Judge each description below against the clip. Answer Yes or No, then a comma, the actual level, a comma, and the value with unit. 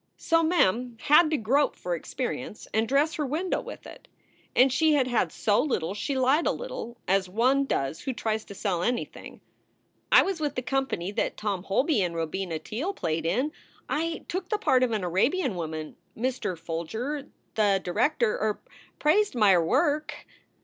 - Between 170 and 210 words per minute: Yes, average, 175 wpm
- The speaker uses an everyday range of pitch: No, wide, 7.2 semitones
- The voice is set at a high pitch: Yes, high, 245 Hz